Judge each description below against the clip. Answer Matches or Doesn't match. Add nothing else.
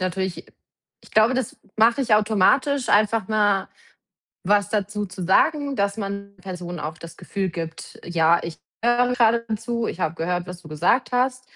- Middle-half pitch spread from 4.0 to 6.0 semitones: Matches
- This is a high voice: Matches